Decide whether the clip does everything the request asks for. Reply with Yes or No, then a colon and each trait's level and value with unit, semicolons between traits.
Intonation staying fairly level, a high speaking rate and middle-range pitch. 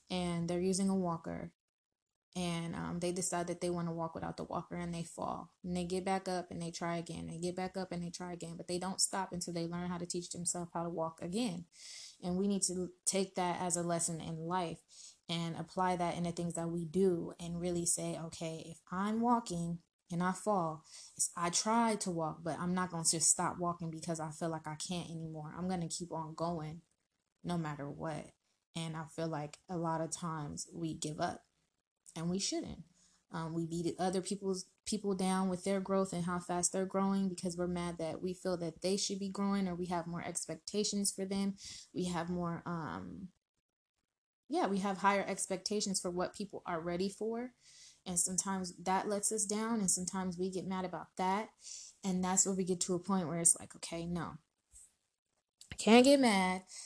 Yes: narrow, 2.1 semitones; fast, 215 wpm; medium, 175 Hz